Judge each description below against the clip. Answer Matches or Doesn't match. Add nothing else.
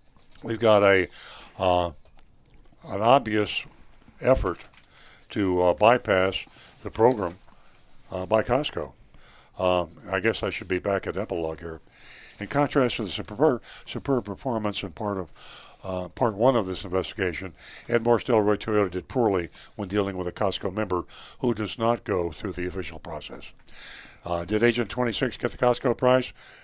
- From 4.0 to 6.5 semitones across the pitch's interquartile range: Matches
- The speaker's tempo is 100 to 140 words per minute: Doesn't match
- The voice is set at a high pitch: Doesn't match